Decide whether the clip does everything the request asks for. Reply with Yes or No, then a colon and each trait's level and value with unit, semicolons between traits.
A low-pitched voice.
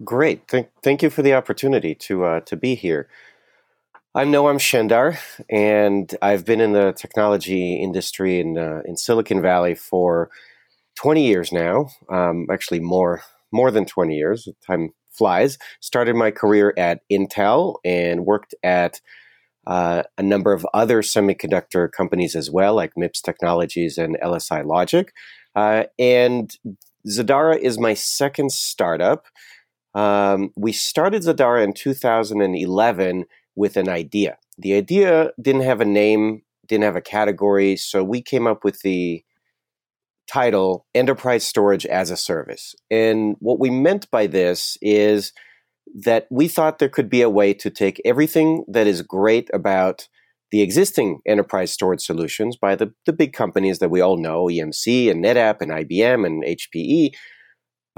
Yes: low, 105 Hz